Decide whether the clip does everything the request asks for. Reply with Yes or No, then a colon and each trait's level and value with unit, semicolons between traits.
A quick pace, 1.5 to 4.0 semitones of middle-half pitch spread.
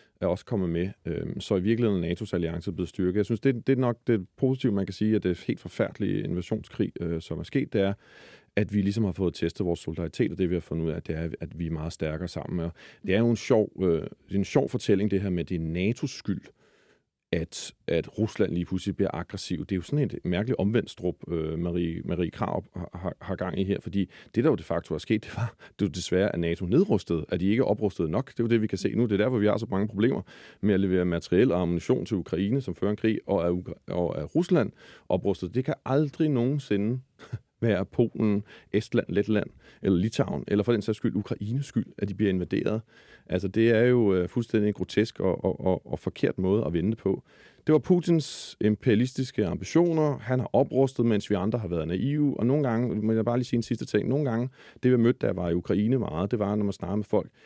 No: fast, 240 wpm; average, 4.6 semitones